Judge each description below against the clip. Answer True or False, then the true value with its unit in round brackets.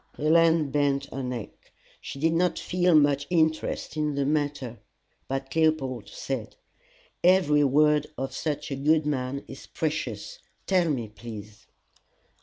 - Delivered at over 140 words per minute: False (135 wpm)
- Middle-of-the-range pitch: True (145 Hz)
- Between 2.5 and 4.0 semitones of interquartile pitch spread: True (2.8 semitones)